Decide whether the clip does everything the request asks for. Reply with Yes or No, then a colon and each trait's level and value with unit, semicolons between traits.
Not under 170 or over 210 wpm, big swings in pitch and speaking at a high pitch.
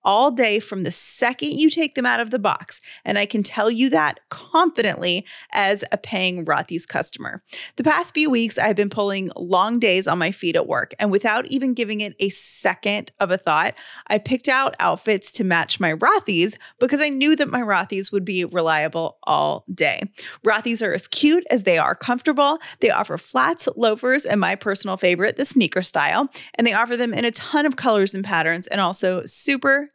Yes: average, 200 wpm; wide, 5.8 semitones; high, 215 Hz